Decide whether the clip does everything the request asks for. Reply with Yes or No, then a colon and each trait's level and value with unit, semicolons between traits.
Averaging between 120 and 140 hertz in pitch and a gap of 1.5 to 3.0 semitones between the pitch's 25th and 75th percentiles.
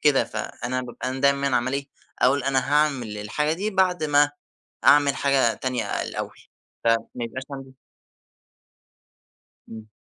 Yes: low, 135 Hz; average, 2.7 semitones